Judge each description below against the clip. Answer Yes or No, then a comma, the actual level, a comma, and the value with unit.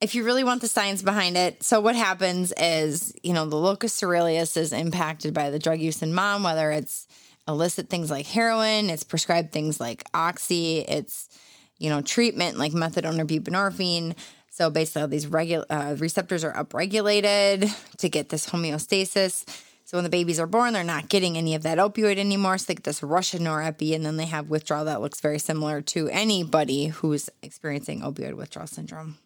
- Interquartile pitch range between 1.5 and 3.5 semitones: No, average, 4.0 semitones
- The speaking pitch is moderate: Yes, medium, 165 Hz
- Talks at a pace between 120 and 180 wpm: No, average, 195 wpm